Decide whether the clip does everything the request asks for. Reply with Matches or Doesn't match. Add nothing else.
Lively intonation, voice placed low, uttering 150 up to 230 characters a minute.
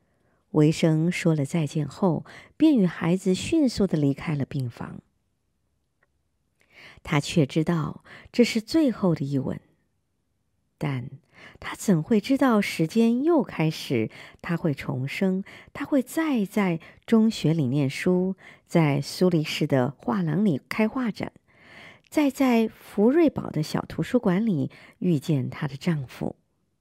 Doesn't match